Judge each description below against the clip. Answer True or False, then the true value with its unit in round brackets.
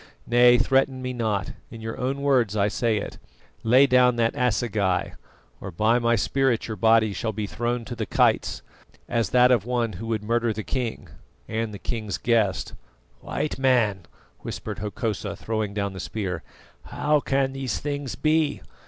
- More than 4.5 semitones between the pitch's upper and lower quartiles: False (2.9 semitones)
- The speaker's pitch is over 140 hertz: False (115 Hz)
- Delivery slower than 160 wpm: False (170 wpm)